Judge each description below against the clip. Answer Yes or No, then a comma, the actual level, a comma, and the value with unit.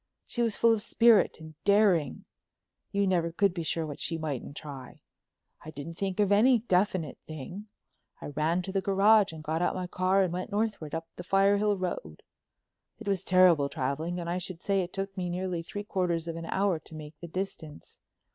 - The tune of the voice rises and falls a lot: No, average, 3.5 semitones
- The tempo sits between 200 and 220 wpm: Yes, fast, 205 wpm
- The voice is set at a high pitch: No, medium, 180 Hz